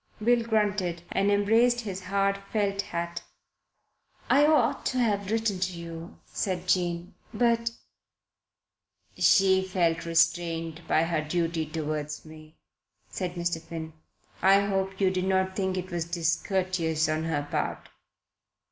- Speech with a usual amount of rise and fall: Yes, average, 3.2 semitones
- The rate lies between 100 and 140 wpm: Yes, slow, 135 wpm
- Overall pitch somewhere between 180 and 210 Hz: Yes, medium, 185 Hz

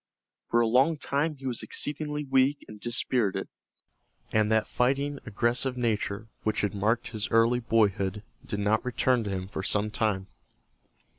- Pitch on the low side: Yes, low, 115 Hz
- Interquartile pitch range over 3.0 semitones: Yes, average, 3.7 semitones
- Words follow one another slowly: No, average, 155 wpm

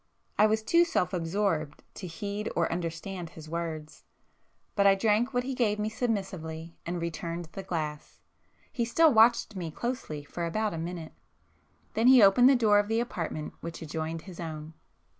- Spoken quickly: No, average, 170 wpm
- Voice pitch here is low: No, medium, 185 Hz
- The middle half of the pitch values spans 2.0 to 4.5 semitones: No, average, 5.1 semitones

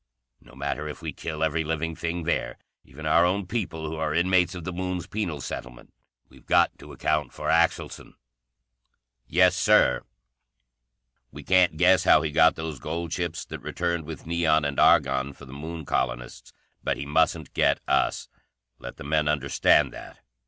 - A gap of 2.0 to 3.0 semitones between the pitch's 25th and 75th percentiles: Yes, average, 2.7 semitones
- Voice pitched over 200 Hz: No, very low, 80 Hz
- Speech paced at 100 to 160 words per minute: No, average, 170 wpm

